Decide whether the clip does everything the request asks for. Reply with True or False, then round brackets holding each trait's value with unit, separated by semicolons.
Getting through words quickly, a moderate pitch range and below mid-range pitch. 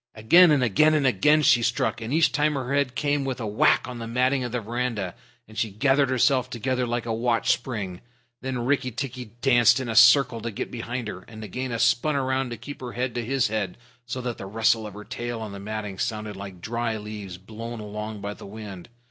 True (225 wpm; 3.2 semitones; 120 Hz)